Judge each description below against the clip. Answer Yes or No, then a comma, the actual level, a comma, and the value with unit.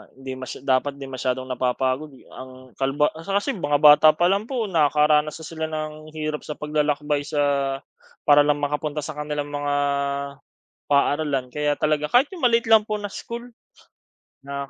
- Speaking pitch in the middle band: Yes, medium, 150 Hz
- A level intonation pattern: Yes, narrow, 2.0 semitones